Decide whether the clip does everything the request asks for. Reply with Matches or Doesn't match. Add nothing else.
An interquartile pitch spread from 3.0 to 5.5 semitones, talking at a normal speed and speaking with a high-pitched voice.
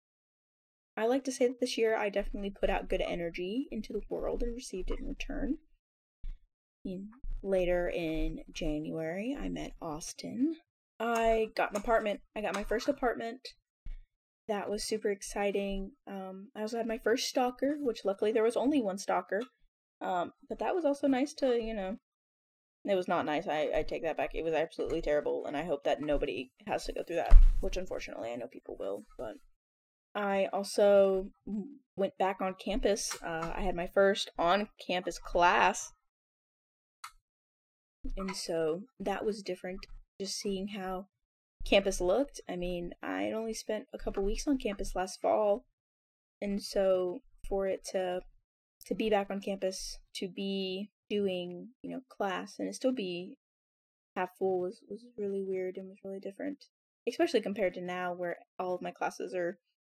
Matches